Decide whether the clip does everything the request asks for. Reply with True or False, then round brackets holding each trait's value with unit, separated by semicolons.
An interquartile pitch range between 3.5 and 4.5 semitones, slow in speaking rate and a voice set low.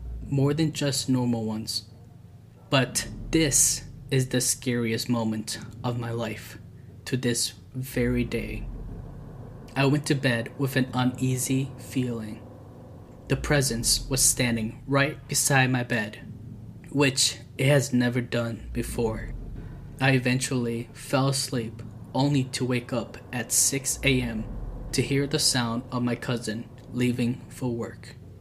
False (2.4 semitones; 130 wpm; 125 Hz)